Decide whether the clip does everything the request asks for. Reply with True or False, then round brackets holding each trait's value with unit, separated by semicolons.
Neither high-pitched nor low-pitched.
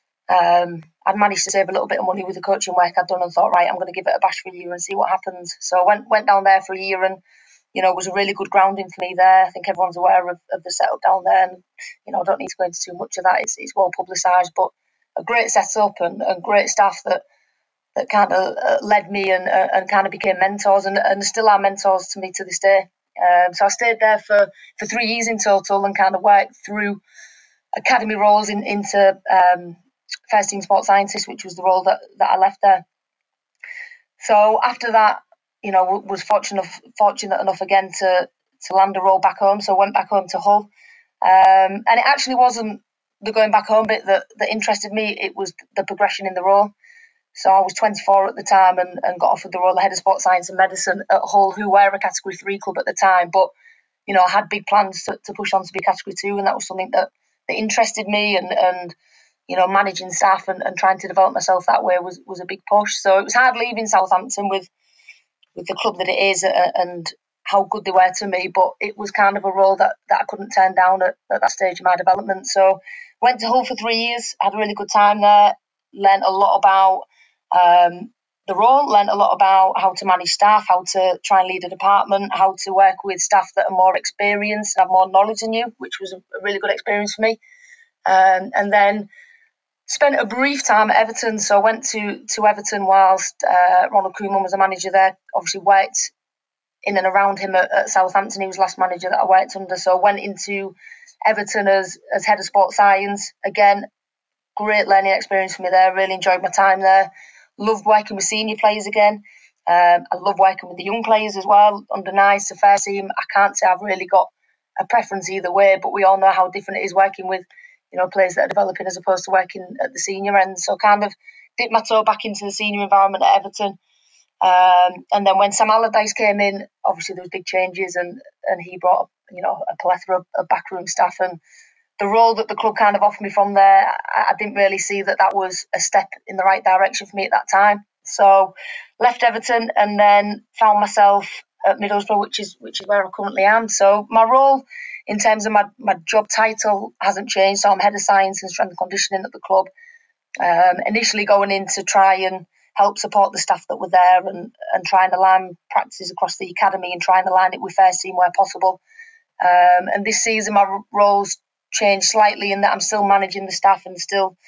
False (195 Hz)